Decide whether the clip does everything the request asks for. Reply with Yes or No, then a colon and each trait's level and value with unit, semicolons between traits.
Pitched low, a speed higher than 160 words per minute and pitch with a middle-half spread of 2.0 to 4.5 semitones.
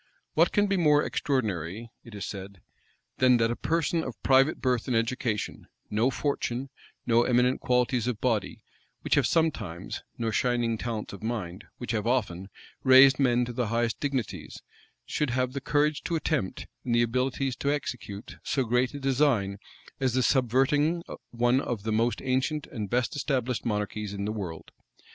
Yes: low, 125 Hz; average, 170 wpm; average, 3.3 semitones